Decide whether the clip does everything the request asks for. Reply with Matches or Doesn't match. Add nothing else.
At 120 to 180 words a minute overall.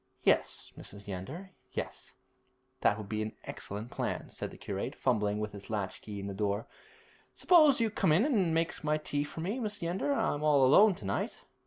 Doesn't match